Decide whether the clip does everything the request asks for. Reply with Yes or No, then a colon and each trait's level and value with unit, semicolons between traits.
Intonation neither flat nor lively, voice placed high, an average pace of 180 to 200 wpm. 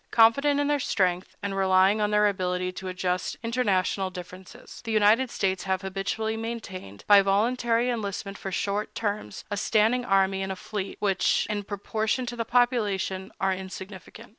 No: average, 3.1 semitones; high, 200 Hz; average, 165 wpm